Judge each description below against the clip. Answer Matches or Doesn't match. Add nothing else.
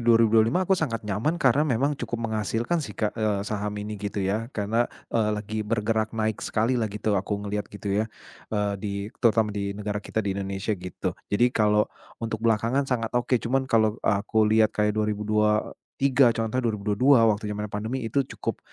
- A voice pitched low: Matches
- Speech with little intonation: Matches